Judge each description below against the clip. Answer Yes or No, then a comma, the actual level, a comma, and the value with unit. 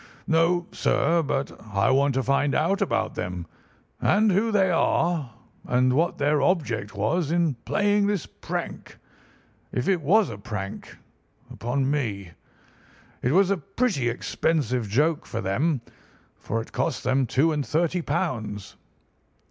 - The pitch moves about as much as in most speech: No, wide, 6.4 semitones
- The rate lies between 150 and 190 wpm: No, slow, 135 wpm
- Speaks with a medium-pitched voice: Yes, medium, 145 Hz